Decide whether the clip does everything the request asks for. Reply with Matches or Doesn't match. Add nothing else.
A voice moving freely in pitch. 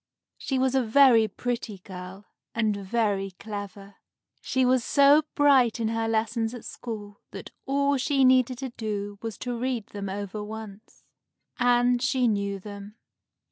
Doesn't match